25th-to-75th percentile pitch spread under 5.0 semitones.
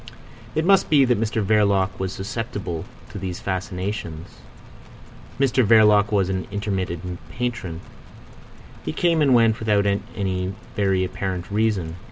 Yes: average, 3.2 semitones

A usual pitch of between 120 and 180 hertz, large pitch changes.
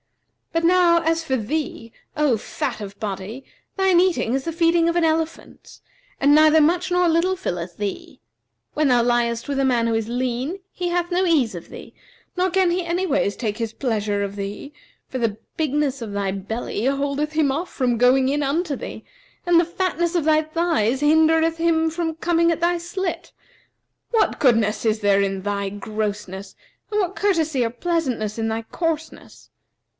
No: very high, 290 Hz; wide, 6.9 semitones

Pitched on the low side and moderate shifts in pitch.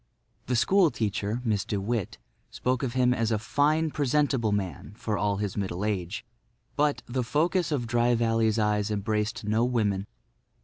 Yes: low, 115 Hz; average, 3.4 semitones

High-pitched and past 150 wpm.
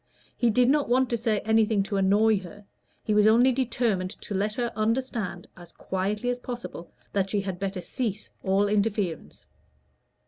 Yes: high, 210 Hz; average, 170 wpm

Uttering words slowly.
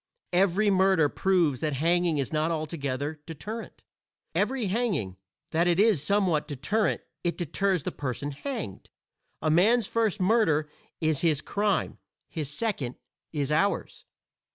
Yes: slow, 130 wpm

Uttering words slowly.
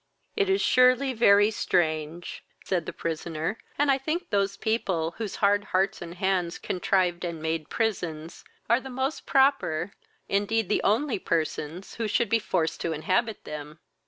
No: average, 160 wpm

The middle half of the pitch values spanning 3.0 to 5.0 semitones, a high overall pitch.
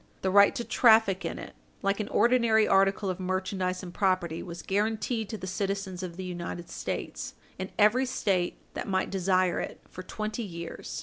No: narrow, 2.5 semitones; high, 195 Hz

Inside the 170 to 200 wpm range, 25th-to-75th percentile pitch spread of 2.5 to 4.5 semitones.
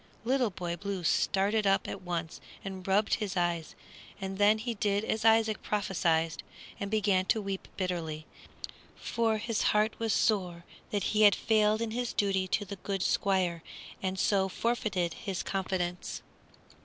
No: average, 155 wpm; average, 2.9 semitones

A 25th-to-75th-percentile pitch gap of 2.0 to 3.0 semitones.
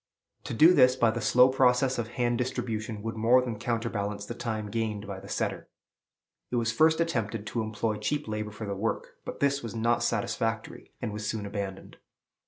Yes: average, 2.7 semitones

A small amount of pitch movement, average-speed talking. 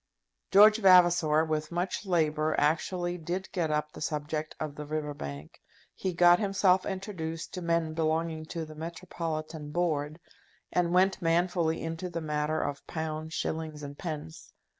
Yes: narrow, 2.3 semitones; average, 150 wpm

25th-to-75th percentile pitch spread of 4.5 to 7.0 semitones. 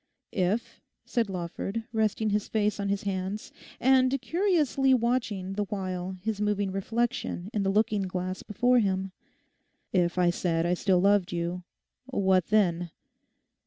No: average, 3.3 semitones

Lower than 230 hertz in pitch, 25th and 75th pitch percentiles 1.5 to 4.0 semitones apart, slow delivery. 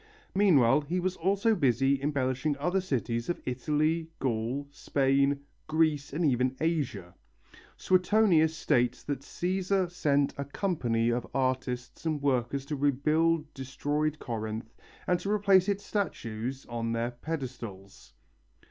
No: medium, 140 Hz; average, 5.0 semitones; slow, 125 wpm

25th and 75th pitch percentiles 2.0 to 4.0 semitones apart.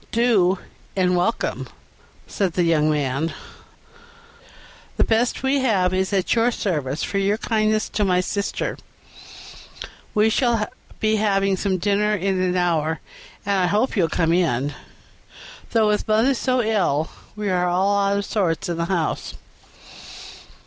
Yes: average, 3.5 semitones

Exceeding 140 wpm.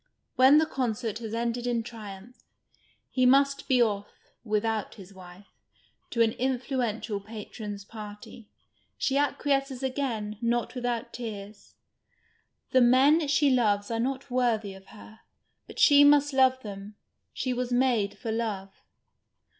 No: slow, 135 wpm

